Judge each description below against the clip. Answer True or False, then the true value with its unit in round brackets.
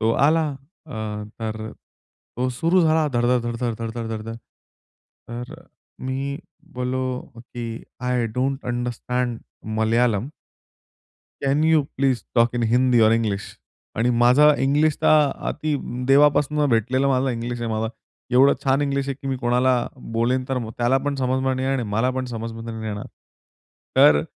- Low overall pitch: True (125 Hz)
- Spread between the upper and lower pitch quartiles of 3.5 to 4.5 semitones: False (2.9 semitones)